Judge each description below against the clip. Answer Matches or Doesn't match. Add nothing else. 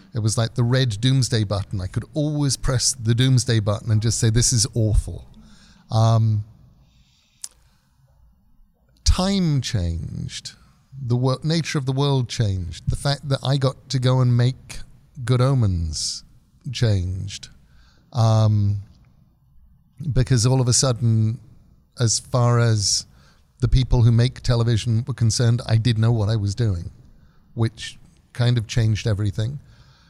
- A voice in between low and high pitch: Doesn't match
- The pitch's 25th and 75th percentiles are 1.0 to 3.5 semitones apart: Matches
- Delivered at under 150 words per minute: Matches